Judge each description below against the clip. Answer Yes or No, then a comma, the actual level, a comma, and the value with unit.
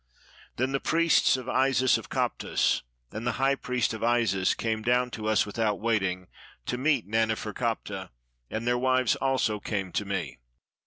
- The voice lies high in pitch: No, low, 115 Hz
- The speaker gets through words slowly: No, average, 165 wpm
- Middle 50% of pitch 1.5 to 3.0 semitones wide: No, average, 3.4 semitones